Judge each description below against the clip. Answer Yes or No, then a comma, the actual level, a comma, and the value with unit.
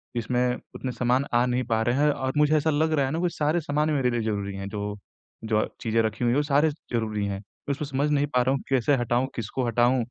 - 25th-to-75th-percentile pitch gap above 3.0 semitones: Yes, average, 4.1 semitones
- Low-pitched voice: Yes, low, 125 Hz